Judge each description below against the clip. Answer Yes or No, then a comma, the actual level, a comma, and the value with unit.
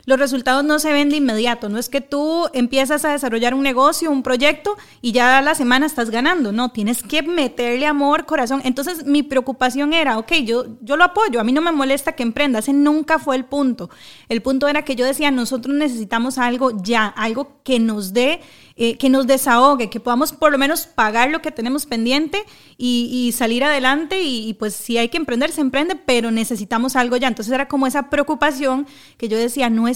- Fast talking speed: Yes, fast, 215 wpm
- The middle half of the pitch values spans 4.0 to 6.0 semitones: No, average, 3.5 semitones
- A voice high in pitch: Yes, very high, 265 Hz